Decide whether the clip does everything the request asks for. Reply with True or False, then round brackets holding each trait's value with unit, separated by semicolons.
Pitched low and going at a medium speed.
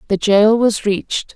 False (210 Hz; 175 wpm)